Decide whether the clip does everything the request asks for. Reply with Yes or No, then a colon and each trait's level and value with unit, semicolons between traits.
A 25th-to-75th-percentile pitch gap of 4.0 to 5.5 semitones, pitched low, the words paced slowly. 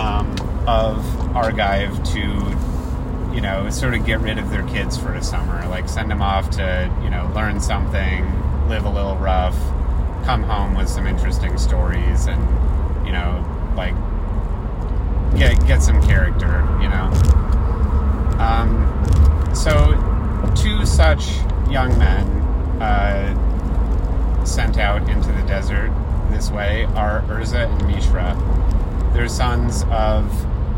Yes: average, 4.6 semitones; very low, 75 Hz; slow, 125 wpm